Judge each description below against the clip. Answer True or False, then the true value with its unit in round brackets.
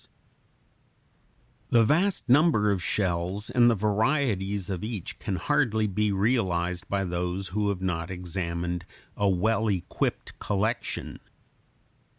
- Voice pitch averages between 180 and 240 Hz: False (100 Hz)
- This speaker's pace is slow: True (130 wpm)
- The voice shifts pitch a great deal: False (3.6 semitones)